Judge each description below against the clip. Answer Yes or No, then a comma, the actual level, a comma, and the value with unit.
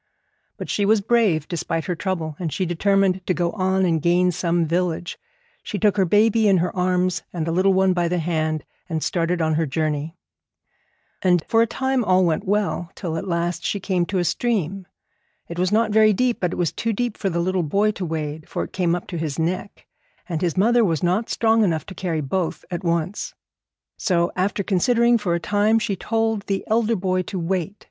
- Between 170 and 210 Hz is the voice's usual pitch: Yes, medium, 185 Hz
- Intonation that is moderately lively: Yes, average, 3.3 semitones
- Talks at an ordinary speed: No, fast, 215 wpm